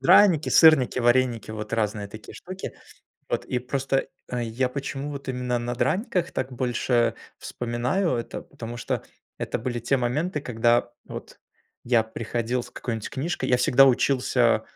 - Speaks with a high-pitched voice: No, low, 125 Hz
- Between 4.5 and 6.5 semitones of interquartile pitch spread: No, narrow, 2.4 semitones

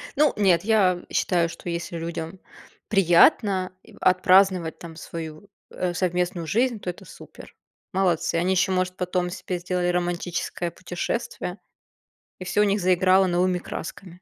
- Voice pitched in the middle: Yes, medium, 180 Hz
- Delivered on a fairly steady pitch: Yes, narrow, 1.6 semitones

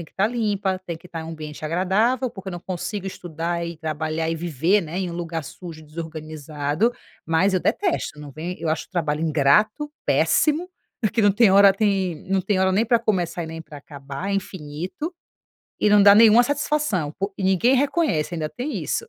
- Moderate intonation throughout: Yes, average, 4.5 semitones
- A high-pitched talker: No, medium, 180 Hz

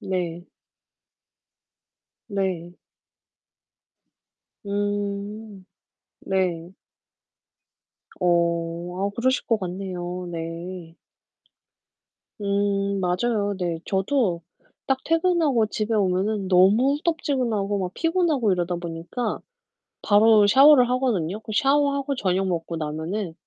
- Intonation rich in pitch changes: No, average, 4.5 semitones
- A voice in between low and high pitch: No, high, 200 Hz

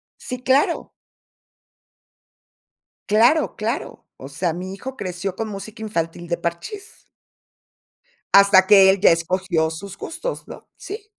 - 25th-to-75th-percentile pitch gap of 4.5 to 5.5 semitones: Yes, average, 4.8 semitones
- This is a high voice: Yes, high, 195 Hz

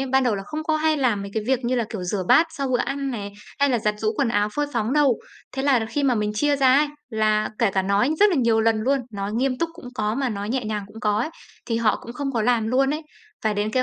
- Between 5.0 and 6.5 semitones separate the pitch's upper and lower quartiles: No, average, 4.3 semitones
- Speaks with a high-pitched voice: Yes, high, 240 Hz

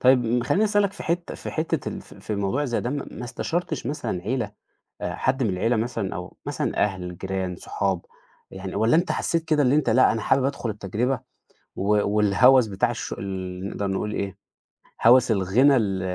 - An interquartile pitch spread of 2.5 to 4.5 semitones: No, average, 5.3 semitones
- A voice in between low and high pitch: No, low, 115 Hz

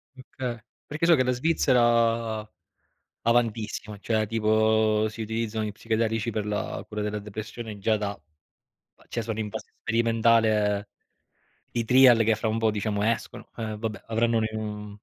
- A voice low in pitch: Yes, low, 110 Hz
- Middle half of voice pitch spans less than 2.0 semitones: Yes, narrow, 1.5 semitones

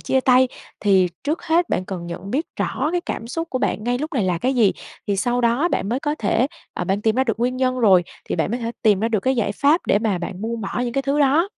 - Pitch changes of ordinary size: Yes, average, 4.7 semitones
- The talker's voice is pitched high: Yes, high, 240 Hz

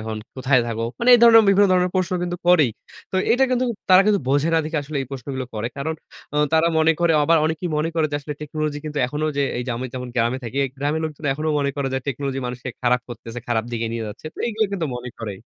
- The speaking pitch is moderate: Yes, medium, 145 Hz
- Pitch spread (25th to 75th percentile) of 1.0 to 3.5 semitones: No, average, 4.9 semitones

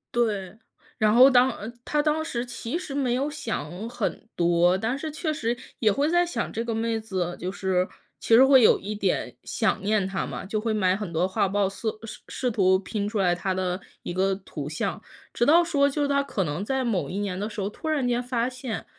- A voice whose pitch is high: Yes, high, 220 Hz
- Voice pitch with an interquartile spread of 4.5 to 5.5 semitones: Yes, average, 5.1 semitones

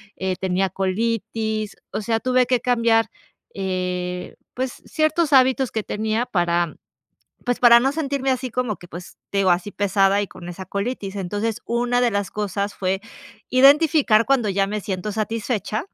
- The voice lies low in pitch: No, high, 215 Hz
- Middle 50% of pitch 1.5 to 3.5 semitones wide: No, average, 4.3 semitones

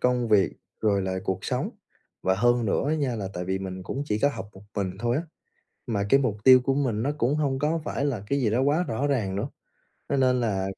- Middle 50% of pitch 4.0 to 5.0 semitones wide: No, wide, 5.5 semitones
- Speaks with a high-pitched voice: No, low, 120 Hz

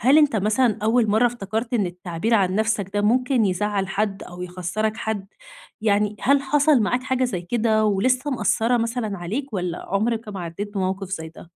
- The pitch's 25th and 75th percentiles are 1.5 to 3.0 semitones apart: No, average, 3.8 semitones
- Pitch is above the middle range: Yes, high, 215 Hz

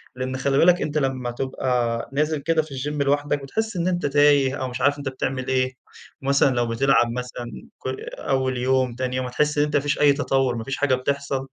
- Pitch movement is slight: Yes, narrow, 2.1 semitones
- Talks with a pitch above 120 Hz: Yes, low, 135 Hz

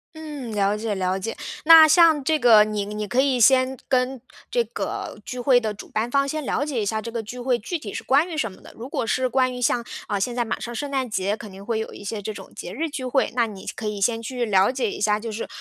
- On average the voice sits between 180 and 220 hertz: No, high, 235 Hz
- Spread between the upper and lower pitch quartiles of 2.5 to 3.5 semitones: No, average, 3.9 semitones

